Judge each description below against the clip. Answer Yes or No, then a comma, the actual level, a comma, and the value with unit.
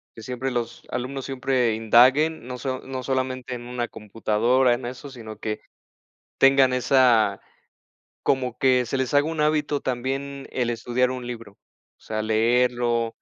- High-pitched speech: No, low, 125 Hz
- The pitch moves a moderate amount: No, narrow, 2.0 semitones